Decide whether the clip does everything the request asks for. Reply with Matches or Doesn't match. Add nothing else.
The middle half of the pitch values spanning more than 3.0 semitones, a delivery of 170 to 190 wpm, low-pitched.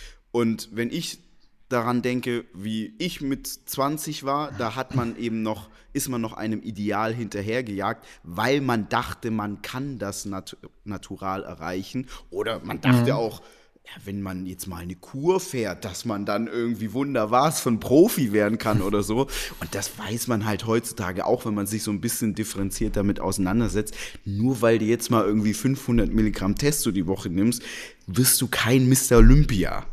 Matches